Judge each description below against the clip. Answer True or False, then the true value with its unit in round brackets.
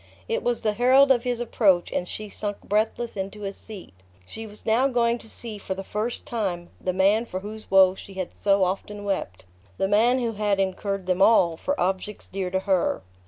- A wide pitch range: False (3.2 semitones)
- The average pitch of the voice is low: False (205 Hz)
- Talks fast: True (210 wpm)